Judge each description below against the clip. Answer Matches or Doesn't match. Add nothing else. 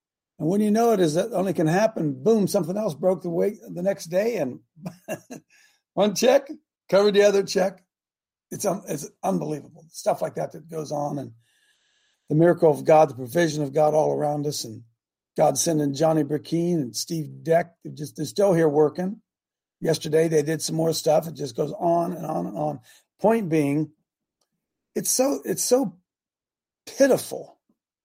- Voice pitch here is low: Doesn't match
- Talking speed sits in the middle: Matches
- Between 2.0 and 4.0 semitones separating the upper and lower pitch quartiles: Doesn't match